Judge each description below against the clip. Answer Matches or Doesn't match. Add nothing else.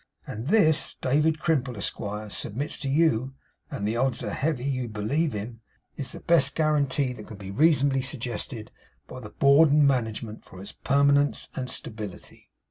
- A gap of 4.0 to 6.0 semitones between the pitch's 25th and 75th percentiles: Matches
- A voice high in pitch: Doesn't match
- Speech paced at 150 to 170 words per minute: Matches